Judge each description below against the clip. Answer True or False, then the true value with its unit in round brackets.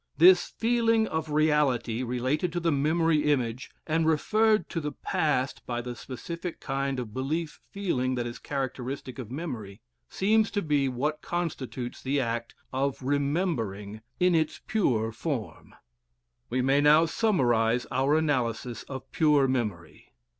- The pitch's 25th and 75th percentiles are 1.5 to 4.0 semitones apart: False (4.7 semitones)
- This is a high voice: False (140 Hz)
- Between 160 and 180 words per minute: False (140 wpm)